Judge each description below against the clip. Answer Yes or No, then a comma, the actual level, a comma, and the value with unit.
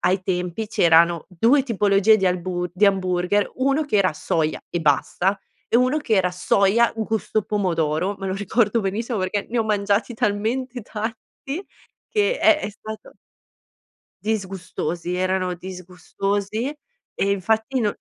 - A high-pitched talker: Yes, high, 200 Hz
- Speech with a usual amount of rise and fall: Yes, average, 3.4 semitones